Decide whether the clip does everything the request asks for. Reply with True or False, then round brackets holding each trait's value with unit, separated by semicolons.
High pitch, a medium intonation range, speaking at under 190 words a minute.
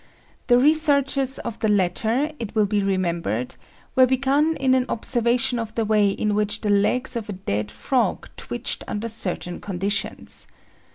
True (220 Hz; 4.4 semitones; 160 wpm)